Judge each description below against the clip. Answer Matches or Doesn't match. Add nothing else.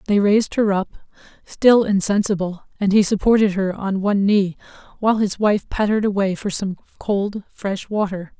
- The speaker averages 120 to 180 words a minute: Matches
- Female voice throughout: Matches